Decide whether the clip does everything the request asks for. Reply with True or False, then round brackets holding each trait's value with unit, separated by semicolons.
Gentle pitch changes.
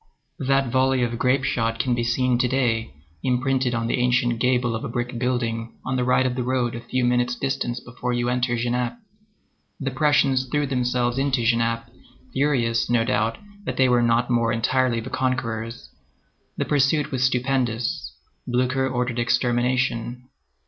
True (1.5 semitones)